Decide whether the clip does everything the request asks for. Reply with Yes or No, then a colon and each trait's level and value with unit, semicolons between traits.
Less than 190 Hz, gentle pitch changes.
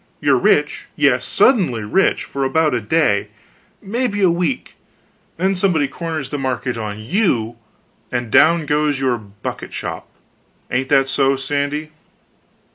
No: medium, 140 Hz; average, 5.2 semitones